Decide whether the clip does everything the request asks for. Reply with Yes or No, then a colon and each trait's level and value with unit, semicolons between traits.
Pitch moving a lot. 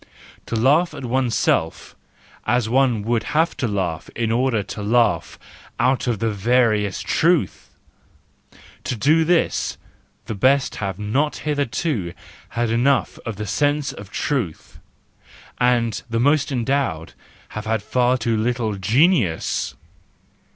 No: average, 4.3 semitones